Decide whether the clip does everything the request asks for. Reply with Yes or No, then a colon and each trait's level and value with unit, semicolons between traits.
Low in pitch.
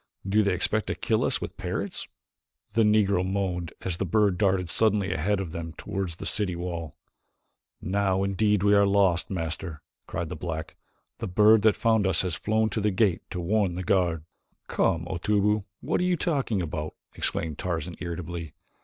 Yes: very low, 95 Hz